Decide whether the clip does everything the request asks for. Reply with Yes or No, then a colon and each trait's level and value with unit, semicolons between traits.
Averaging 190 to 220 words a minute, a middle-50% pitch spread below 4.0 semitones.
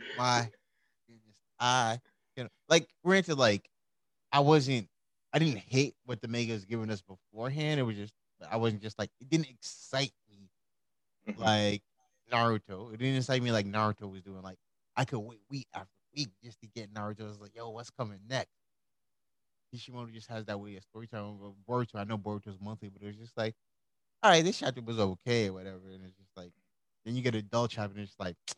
Yes: fast, 205 wpm; average, 3.4 semitones